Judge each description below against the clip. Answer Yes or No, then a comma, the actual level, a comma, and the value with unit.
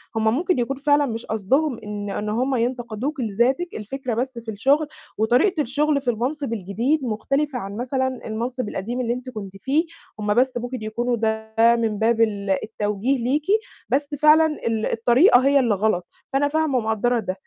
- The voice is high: Yes, high, 240 Hz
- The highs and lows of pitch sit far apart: No, average, 3.8 semitones